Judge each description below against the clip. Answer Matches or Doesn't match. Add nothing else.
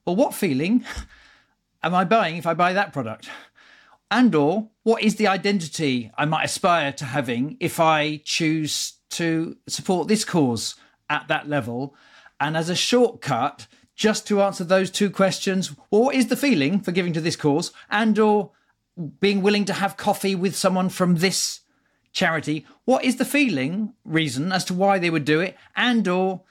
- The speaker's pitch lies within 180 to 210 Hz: Matches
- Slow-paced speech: Doesn't match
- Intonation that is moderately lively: Matches